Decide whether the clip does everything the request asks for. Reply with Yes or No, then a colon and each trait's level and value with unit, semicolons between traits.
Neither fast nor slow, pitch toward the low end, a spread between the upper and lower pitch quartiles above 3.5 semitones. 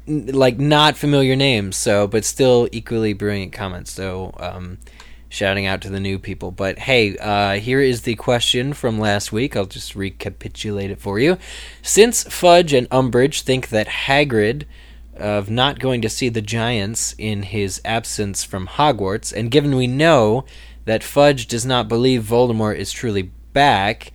Yes: average, 165 wpm; low, 110 Hz; average, 4.6 semitones